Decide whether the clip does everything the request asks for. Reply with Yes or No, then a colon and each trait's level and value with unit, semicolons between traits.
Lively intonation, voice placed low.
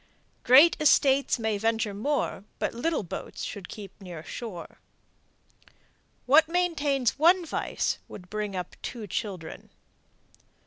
No: wide, 6.4 semitones; high, 230 Hz